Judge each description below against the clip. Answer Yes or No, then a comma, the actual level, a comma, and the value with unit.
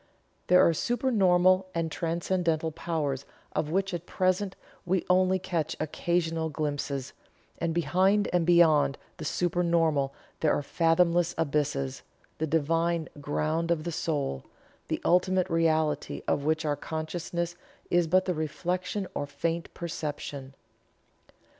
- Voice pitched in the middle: Yes, medium, 165 Hz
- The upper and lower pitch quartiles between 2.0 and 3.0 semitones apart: Yes, narrow, 2.5 semitones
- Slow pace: Yes, slow, 125 wpm